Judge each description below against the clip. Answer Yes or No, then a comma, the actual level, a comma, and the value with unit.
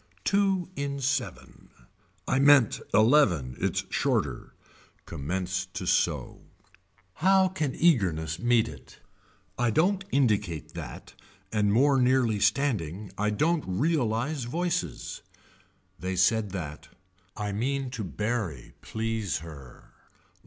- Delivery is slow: Yes, slow, 110 wpm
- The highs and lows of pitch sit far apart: Yes, wide, 7.2 semitones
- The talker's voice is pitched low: Yes, low, 115 Hz